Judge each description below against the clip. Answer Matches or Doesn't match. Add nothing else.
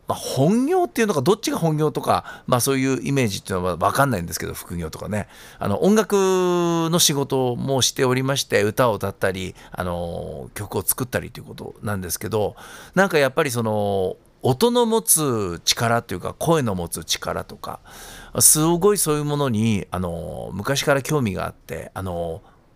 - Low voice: Matches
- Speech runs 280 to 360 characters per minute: Matches